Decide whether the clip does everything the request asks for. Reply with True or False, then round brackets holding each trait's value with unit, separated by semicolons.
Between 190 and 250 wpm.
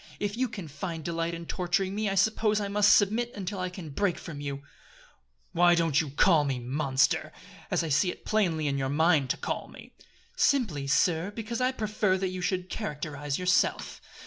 True (195 wpm)